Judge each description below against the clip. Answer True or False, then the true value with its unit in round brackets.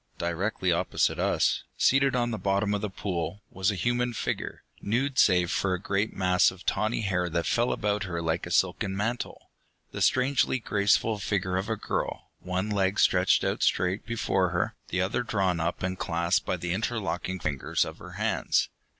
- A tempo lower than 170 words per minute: False (185 wpm)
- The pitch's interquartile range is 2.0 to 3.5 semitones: True (3.2 semitones)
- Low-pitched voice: True (95 Hz)